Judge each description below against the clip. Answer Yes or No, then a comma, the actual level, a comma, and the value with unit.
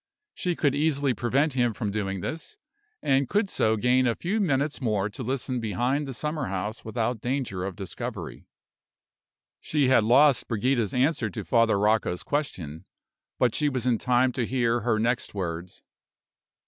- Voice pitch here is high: No, low, 120 Hz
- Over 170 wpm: No, average, 160 wpm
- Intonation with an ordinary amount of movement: Yes, average, 4.2 semitones